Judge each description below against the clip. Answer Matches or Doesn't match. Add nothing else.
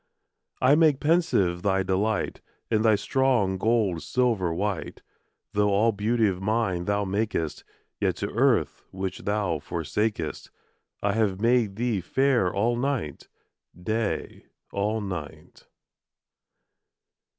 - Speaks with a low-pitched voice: Matches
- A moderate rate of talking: Doesn't match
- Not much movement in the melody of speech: Doesn't match